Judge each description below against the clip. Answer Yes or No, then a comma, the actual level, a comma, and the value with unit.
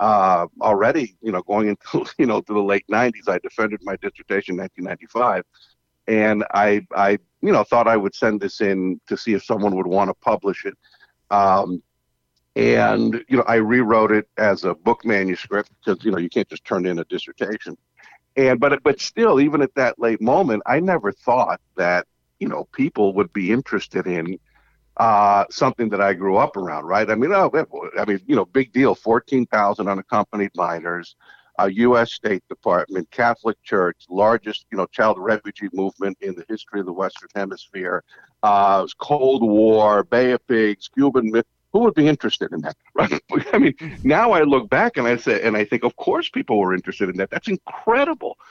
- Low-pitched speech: Yes, low, 105 Hz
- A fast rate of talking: No, average, 190 wpm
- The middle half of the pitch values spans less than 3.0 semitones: No, average, 3.4 semitones